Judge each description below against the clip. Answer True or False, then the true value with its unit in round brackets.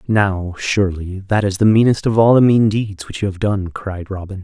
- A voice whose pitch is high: False (100 Hz)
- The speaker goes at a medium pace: False (230 wpm)